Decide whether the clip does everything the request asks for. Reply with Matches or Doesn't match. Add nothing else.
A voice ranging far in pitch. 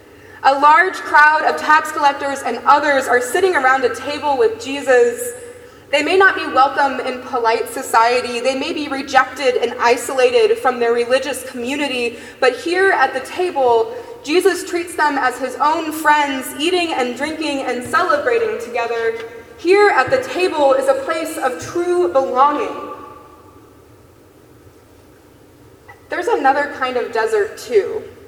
Matches